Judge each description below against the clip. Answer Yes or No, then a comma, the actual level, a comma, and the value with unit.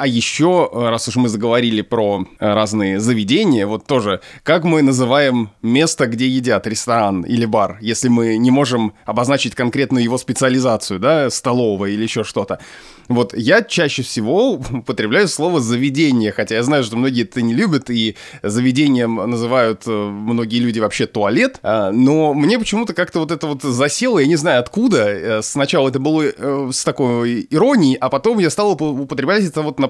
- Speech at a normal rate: No, fast, 165 wpm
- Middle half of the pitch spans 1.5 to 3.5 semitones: No, average, 4.0 semitones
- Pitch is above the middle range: No, low, 130 Hz